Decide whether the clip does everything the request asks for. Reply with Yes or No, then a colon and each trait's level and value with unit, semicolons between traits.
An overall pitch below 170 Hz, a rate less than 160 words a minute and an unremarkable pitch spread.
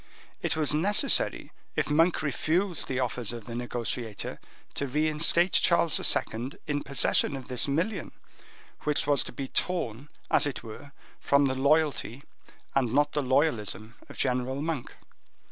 Yes: medium, 140 Hz; average, 150 wpm; average, 3.7 semitones